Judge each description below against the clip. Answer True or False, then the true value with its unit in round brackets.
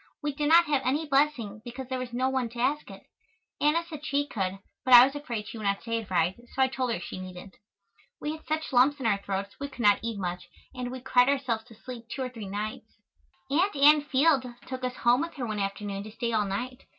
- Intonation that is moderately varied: True (4.6 semitones)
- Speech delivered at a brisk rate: True (245 wpm)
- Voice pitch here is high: True (250 Hz)